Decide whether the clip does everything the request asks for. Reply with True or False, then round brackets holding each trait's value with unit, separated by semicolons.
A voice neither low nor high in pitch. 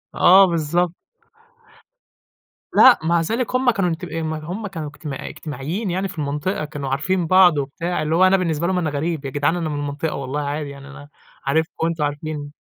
True (160 Hz)